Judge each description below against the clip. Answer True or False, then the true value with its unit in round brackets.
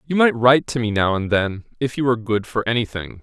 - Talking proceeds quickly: True (280 wpm)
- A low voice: True (115 Hz)